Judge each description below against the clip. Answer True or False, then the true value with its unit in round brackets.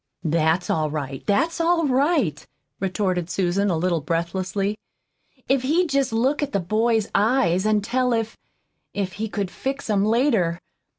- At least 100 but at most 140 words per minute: False (155 wpm)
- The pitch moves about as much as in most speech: False (6.4 semitones)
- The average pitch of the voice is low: False (205 Hz)